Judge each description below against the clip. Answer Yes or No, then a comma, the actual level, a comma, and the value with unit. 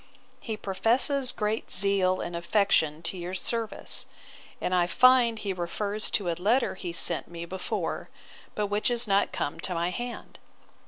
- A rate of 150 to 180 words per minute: Yes, average, 160 wpm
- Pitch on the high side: Yes, high, 200 Hz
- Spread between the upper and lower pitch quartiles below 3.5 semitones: No, average, 4.2 semitones